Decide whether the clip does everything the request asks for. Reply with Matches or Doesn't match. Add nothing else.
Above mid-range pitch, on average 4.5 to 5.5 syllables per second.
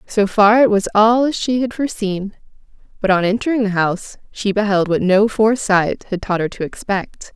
Matches